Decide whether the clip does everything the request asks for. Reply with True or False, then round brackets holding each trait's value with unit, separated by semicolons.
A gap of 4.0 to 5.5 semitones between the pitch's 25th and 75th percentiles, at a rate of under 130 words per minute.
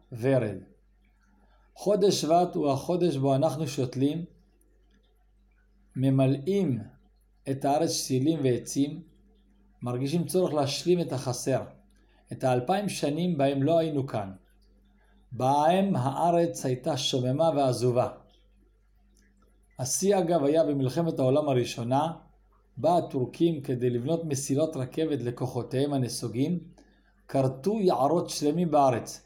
True (4.4 semitones; 100 wpm)